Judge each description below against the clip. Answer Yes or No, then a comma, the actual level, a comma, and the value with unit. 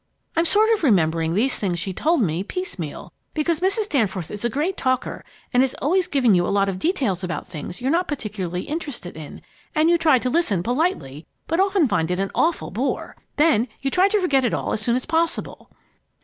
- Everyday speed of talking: No, fast, 210 wpm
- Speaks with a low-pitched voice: No, very high, 255 Hz